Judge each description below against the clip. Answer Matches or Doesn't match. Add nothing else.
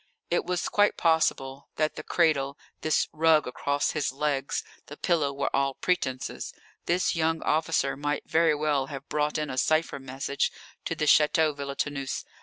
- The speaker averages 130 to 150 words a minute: Doesn't match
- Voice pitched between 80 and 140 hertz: Doesn't match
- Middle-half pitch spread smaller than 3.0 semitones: Matches